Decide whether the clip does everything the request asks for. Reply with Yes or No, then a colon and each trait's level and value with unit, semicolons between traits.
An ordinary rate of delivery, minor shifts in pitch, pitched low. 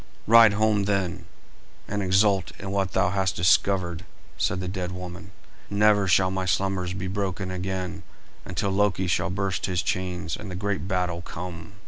Yes: average, 160 wpm; narrow, 1.6 semitones; very low, 95 Hz